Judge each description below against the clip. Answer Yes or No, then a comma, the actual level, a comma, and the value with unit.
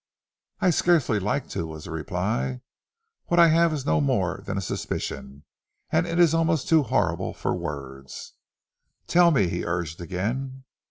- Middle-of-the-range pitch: No, low, 105 Hz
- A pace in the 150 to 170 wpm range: Yes, average, 160 wpm